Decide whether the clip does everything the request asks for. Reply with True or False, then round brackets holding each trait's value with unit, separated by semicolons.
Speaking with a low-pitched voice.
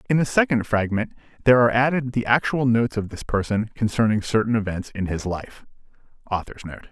True (115 Hz)